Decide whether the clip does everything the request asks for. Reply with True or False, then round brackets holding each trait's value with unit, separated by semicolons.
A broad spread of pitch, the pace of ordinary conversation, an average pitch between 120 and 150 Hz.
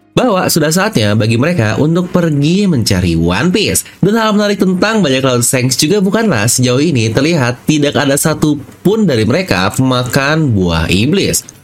True (7.3 semitones; 155 wpm; 140 Hz)